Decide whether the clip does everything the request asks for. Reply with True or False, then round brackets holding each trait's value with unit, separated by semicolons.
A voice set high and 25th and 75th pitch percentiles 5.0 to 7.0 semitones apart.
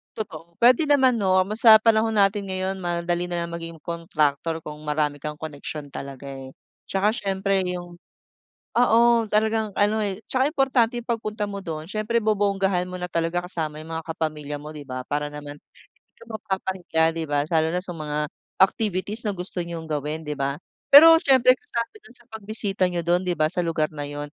False (180 Hz; 5.4 semitones)